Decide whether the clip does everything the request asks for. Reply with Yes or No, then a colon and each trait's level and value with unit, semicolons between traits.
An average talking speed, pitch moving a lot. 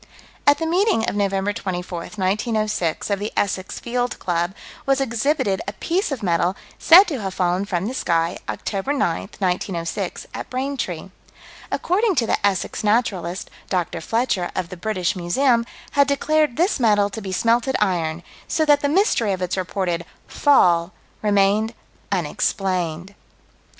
Yes: average, 150 wpm; wide, 5.7 semitones